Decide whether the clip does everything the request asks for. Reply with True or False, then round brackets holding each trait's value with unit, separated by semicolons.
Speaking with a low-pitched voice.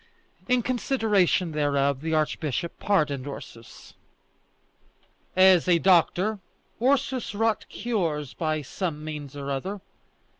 False (170 Hz)